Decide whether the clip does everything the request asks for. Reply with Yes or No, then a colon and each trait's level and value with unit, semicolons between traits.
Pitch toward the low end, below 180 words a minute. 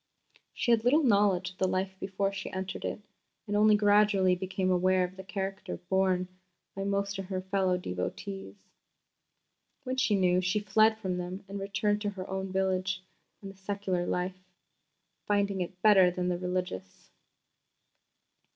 No: high, 190 Hz; average, 160 wpm